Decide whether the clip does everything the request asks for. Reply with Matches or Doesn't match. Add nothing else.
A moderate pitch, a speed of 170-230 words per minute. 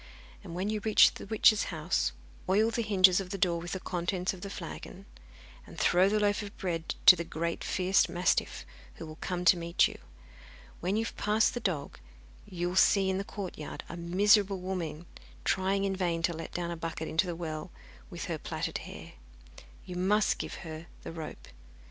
Matches